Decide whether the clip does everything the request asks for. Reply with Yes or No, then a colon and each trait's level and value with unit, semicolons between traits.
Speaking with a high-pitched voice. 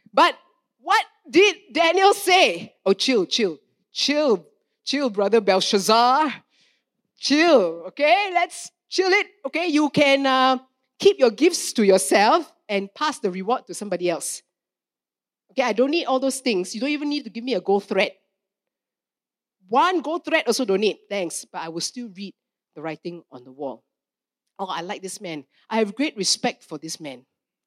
Yes: very high, 250 Hz